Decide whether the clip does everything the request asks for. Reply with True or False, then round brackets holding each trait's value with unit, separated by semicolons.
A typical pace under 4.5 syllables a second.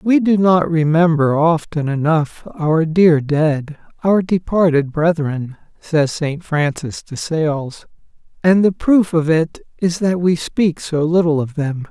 True (3.6 syllables/s)